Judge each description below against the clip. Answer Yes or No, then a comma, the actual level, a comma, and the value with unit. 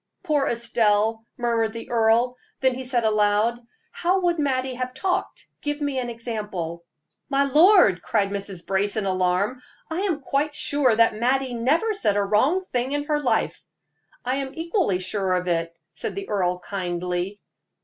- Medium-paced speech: Yes, average, 165 wpm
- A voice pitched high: Yes, high, 235 Hz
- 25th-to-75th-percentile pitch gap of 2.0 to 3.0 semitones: No, wide, 5.6 semitones